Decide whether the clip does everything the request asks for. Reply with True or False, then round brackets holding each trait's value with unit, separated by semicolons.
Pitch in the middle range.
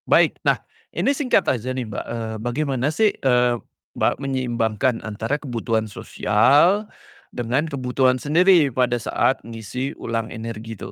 False (125 Hz)